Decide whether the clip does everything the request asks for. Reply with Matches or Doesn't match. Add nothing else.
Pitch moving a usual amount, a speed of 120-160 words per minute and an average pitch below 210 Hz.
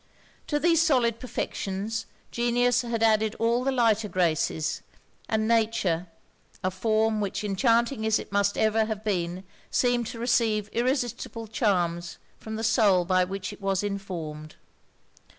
Doesn't match